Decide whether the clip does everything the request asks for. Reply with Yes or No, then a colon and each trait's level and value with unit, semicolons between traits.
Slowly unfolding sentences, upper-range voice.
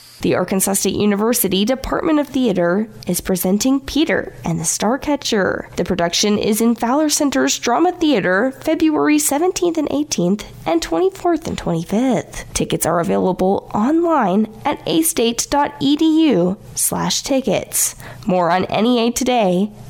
Yes: slow, 125 wpm; high, 235 Hz